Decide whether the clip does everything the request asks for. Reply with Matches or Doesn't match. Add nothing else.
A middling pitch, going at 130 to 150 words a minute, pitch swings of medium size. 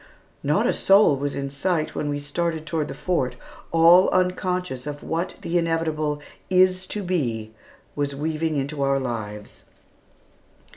Matches